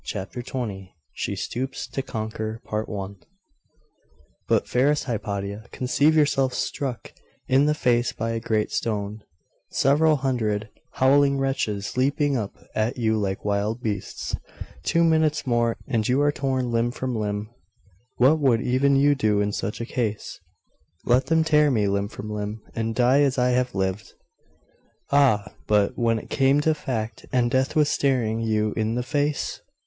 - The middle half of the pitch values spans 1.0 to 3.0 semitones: No, average, 4.0 semitones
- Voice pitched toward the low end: Yes, low, 120 Hz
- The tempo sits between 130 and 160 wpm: Yes, average, 155 wpm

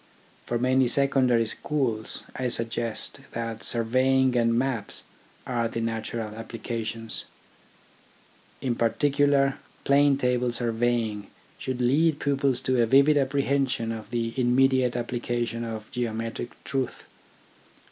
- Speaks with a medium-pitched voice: No, low, 120 Hz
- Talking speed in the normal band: No, slow, 110 wpm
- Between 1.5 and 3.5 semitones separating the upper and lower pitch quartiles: Yes, narrow, 2.5 semitones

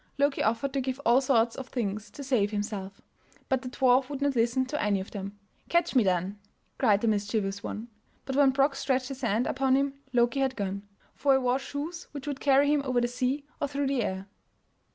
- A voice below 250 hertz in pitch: No, very high, 255 Hz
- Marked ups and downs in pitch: No, average, 4.5 semitones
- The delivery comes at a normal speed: No, fast, 215 wpm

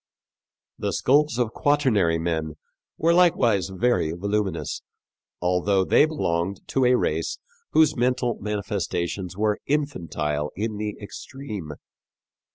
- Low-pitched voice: Yes, low, 105 Hz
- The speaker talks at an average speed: No, slow, 110 wpm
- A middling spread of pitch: No, wide, 6.3 semitones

